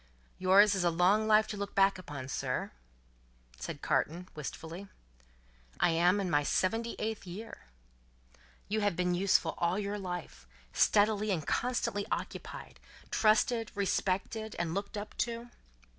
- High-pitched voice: Yes, high, 195 Hz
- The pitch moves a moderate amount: Yes, average, 3.4 semitones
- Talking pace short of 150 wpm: Yes, average, 140 wpm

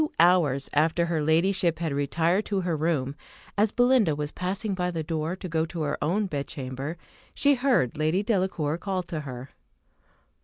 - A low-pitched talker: No, medium, 165 Hz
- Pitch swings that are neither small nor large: Yes, average, 4.0 semitones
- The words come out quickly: No, average, 175 wpm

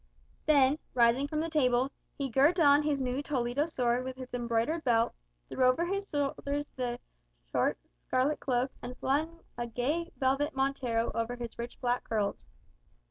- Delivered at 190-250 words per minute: No, average, 160 wpm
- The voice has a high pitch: Yes, very high, 260 Hz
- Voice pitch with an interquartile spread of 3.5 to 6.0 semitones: No, average, 3.1 semitones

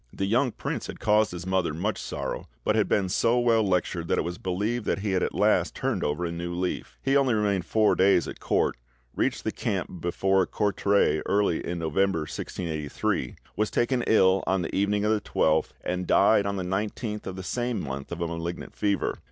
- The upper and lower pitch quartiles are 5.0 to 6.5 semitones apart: No, average, 3.5 semitones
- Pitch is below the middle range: Yes, very low, 95 Hz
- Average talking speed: No, fast, 210 wpm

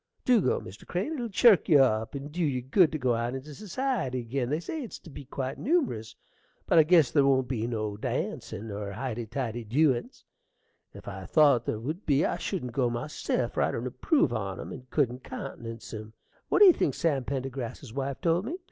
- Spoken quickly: Yes, fast, 210 wpm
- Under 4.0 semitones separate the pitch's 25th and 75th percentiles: No, wide, 5.4 semitones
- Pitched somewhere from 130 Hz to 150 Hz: Yes, low, 135 Hz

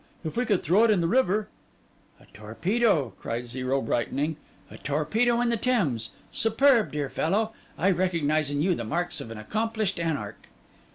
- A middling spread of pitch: No, wide, 7.9 semitones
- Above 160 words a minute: Yes, average, 170 wpm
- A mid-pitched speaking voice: Yes, medium, 170 Hz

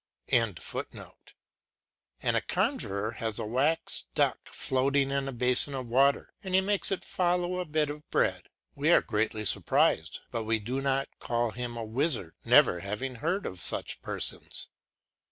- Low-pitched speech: Yes, low, 130 Hz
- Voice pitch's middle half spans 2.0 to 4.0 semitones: No, average, 4.9 semitones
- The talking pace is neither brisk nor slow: Yes, average, 160 wpm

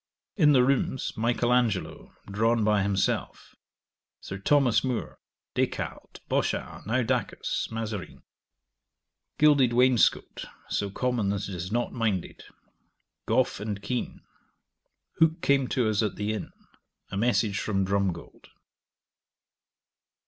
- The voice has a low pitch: Yes, low, 115 Hz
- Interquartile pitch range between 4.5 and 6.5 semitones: No, average, 3.9 semitones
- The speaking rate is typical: No, slow, 115 wpm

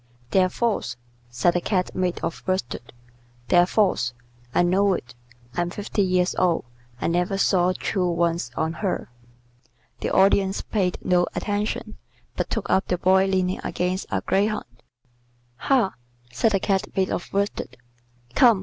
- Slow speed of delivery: No, average, 150 wpm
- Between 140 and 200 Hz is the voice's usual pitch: Yes, medium, 185 Hz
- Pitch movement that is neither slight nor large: No, narrow, 2.1 semitones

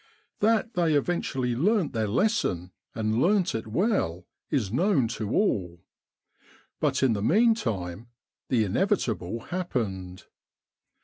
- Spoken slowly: Yes, slow, 115 wpm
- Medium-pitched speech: No, low, 125 Hz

